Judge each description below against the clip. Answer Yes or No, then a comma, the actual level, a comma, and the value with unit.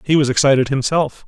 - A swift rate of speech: No, average, 190 wpm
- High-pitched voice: No, medium, 140 Hz